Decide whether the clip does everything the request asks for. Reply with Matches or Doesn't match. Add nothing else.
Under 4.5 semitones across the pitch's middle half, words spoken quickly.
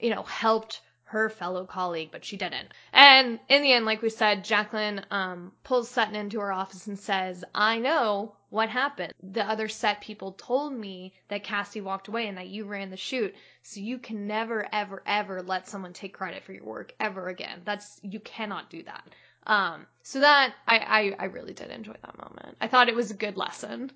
Matches